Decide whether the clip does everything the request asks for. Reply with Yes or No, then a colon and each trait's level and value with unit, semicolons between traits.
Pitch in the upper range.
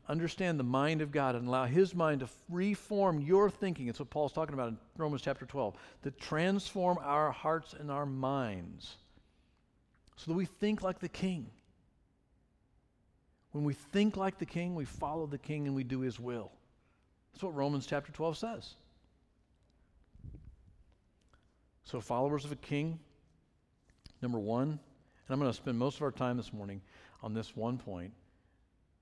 No: medium, 140 Hz